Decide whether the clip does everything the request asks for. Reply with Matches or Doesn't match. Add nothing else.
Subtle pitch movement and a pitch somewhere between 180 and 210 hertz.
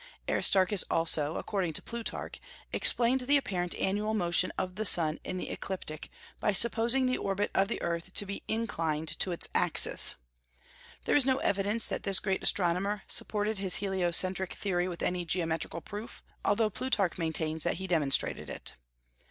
Doesn't match